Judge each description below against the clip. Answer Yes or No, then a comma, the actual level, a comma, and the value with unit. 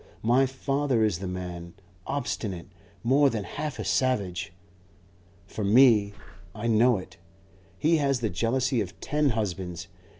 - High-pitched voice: No, low, 115 Hz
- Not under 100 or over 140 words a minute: Yes, slow, 135 wpm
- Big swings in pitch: Yes, wide, 5.8 semitones